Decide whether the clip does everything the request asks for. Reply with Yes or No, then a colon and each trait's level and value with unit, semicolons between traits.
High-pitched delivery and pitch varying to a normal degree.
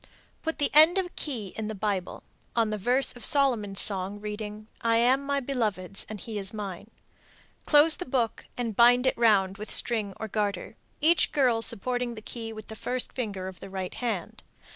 Yes: high, 225 Hz; average, 3.6 semitones